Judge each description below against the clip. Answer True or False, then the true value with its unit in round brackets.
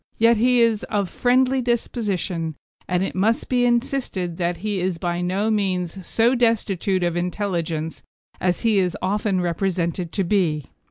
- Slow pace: False (155 wpm)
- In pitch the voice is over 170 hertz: True (190 Hz)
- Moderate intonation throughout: True (4.4 semitones)